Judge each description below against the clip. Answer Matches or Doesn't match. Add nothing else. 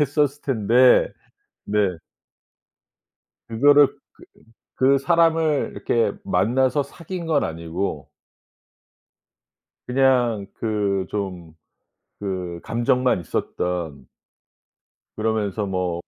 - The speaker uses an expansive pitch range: Matches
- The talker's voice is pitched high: Doesn't match